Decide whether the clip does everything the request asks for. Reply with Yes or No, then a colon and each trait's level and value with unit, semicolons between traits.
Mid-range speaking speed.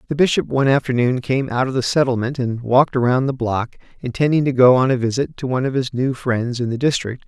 No: fast, 240 wpm